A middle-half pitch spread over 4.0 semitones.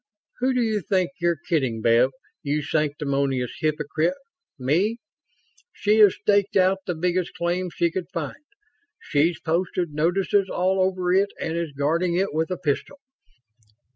No: average, 3.7 semitones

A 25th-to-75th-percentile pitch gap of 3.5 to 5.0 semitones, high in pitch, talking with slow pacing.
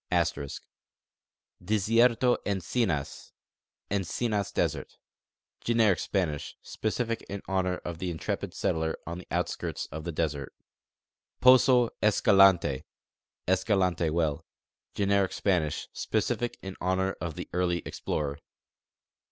No: average, 4.1 semitones; very low, 95 Hz; slow, 105 wpm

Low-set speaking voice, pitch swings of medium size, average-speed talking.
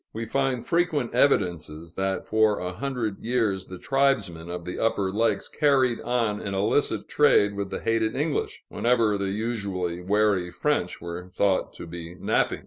Yes: low, 105 Hz; average, 5.0 semitones; average, 160 wpm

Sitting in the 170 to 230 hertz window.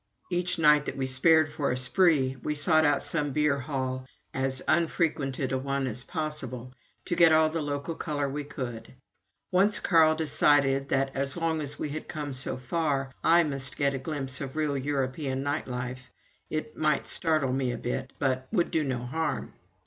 No: medium, 140 Hz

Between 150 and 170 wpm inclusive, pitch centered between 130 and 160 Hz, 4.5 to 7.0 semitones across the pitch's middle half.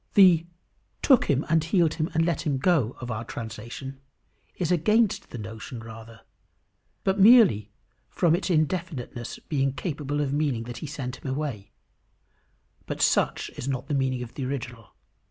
Yes: average, 160 wpm; medium, 140 Hz; wide, 5.5 semitones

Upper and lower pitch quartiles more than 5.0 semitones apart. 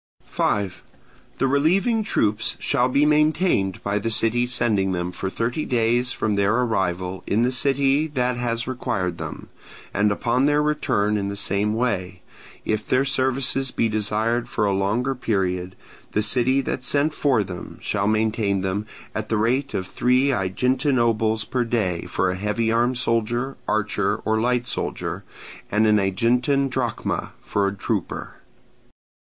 No: average, 4.0 semitones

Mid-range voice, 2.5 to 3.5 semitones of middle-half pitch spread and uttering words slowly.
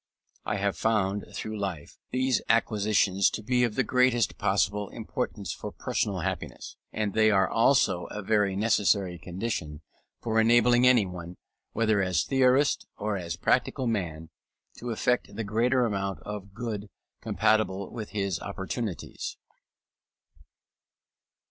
No: low, 105 Hz; average, 3.1 semitones; slow, 130 wpm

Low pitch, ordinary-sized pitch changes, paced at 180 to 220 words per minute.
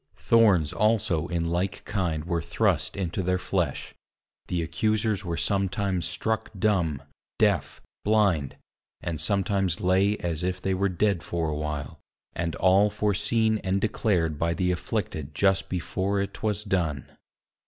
No: very low, 95 Hz; average, 3.3 semitones; average, 145 wpm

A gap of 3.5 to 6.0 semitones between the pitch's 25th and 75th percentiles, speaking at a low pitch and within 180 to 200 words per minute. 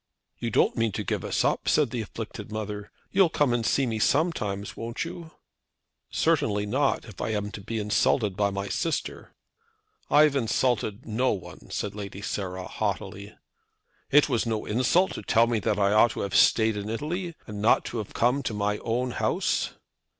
Yes: average, 3.8 semitones; low, 110 Hz; average, 185 wpm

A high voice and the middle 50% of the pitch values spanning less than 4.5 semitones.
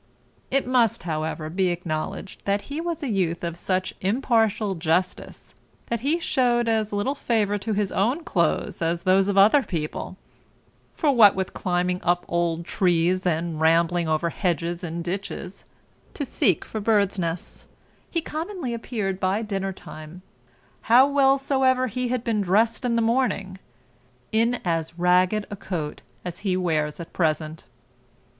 No: high, 195 Hz; average, 5.3 semitones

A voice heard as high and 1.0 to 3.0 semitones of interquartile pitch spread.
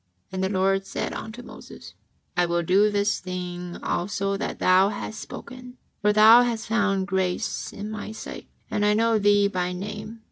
Yes: high, 200 Hz; narrow, 2.5 semitones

